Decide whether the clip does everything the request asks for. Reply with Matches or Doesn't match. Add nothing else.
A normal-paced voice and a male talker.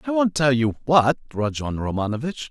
Matches